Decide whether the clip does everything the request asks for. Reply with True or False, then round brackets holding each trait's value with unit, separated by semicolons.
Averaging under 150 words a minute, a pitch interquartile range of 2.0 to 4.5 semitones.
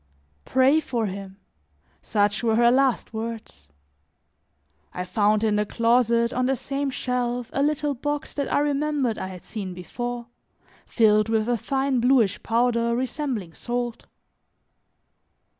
True (135 wpm; 3.6 semitones)